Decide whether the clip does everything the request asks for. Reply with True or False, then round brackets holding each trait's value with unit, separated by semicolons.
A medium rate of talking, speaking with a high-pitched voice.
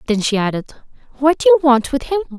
False (225 wpm; 265 Hz)